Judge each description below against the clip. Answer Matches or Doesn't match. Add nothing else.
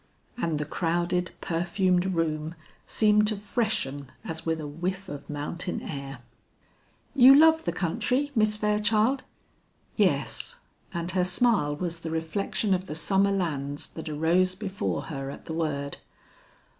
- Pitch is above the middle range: Doesn't match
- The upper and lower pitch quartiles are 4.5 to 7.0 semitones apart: Matches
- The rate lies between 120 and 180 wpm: Matches